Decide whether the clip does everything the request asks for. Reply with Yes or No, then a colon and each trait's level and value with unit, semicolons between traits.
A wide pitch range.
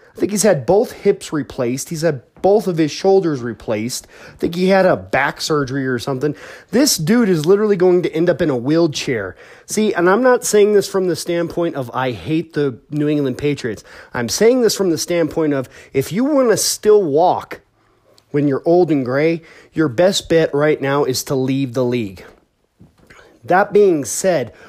Yes: wide, 5.7 semitones